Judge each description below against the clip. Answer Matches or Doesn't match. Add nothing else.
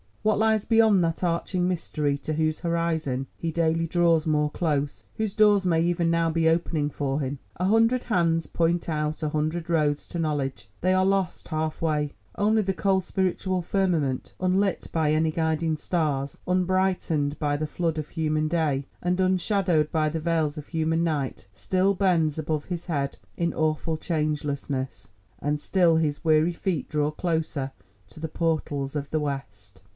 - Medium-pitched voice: Matches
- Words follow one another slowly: Doesn't match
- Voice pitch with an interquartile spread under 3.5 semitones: Matches